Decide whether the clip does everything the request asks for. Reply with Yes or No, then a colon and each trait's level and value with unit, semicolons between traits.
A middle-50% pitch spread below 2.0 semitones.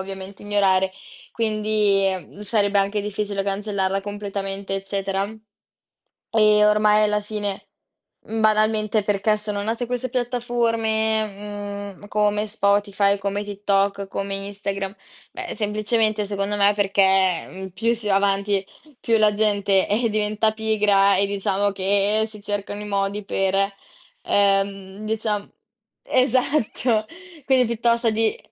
Yes: narrow, 1.5 semitones